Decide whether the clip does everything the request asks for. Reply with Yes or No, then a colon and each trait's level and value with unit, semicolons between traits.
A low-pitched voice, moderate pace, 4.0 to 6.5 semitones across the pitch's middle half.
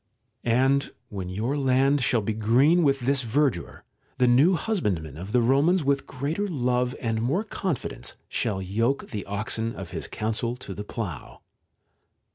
Yes: low, 125 Hz; average, 155 wpm; average, 4.6 semitones